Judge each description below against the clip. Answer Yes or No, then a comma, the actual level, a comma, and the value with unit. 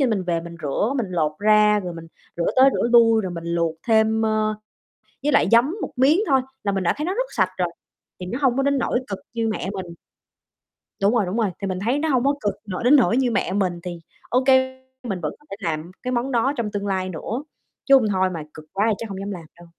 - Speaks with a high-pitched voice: Yes, high, 210 Hz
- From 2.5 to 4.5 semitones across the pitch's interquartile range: No, average, 5.2 semitones